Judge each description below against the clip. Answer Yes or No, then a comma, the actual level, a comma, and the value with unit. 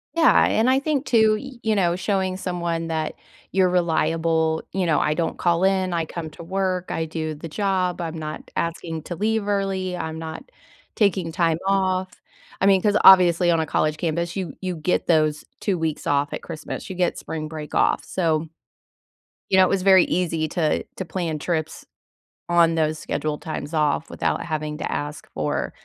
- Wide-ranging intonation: No, average, 3.0 semitones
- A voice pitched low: No, medium, 170 Hz